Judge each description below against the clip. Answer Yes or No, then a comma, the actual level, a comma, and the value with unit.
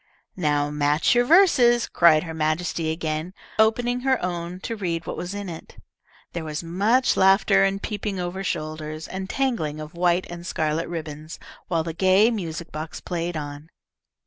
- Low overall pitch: No, medium, 175 Hz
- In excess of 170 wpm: No, average, 165 wpm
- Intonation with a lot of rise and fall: No, average, 4.0 semitones